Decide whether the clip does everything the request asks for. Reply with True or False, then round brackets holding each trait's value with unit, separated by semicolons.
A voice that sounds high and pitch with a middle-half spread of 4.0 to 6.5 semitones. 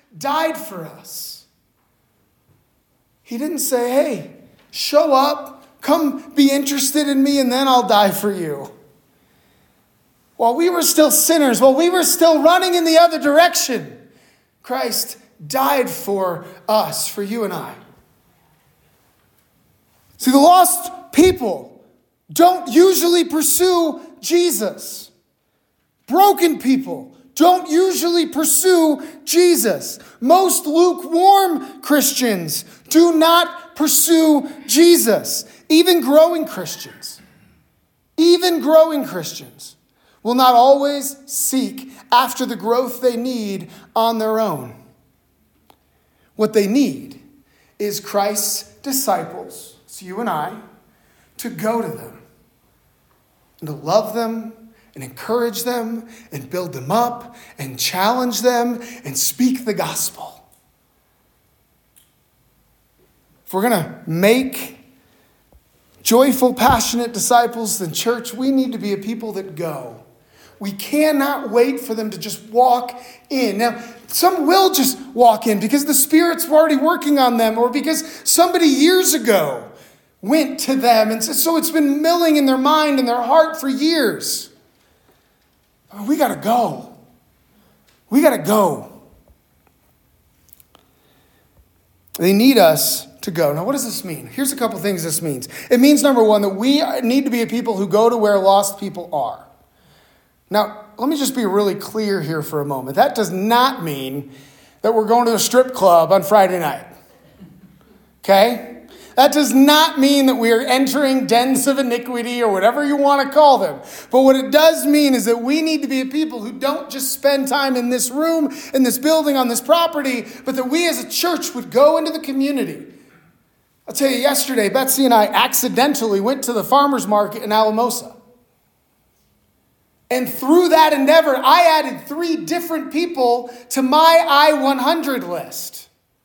True (260 Hz; 5.4 semitones)